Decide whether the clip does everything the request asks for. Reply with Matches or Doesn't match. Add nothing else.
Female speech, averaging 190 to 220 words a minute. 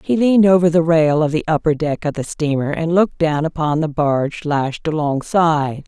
Matches